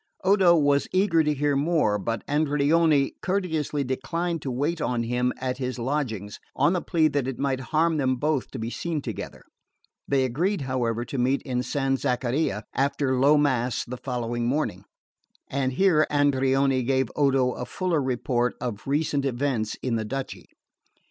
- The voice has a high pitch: No, low, 135 Hz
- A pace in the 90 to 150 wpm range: No, average, 165 wpm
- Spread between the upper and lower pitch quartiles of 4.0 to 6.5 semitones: No, average, 3.2 semitones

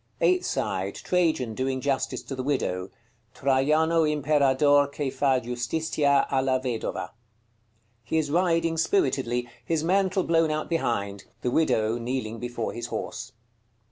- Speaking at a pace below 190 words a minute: Yes, slow, 135 wpm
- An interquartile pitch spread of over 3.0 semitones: Yes, average, 4.6 semitones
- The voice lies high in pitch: No, medium, 140 Hz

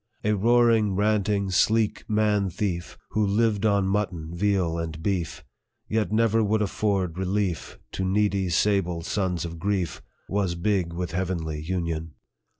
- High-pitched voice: No, very low, 95 Hz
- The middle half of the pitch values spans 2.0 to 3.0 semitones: No, average, 3.4 semitones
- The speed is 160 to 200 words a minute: No, average, 140 wpm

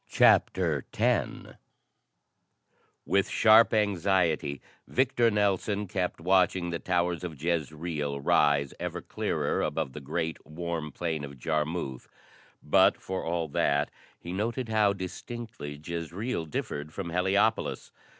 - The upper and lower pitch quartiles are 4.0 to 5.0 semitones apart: Yes, average, 4.3 semitones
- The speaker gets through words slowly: Yes, slow, 115 wpm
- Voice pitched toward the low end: Yes, very low, 85 Hz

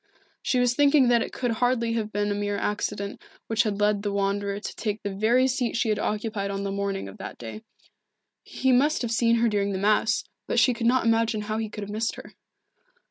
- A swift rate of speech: Yes, fast, 230 wpm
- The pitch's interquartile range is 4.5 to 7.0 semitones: No, narrow, 2.6 semitones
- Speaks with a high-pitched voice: Yes, high, 215 Hz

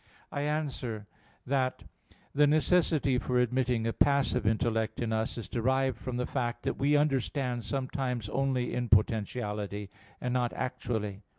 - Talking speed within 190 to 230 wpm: No, average, 140 wpm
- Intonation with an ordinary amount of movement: Yes, average, 3.3 semitones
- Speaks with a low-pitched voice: Yes, low, 125 Hz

